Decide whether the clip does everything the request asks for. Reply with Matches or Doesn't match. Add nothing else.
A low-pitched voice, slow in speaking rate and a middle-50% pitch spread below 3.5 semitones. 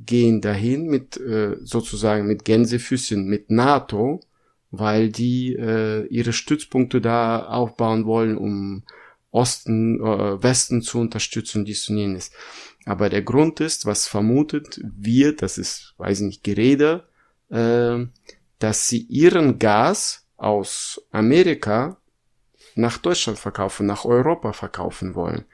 Matches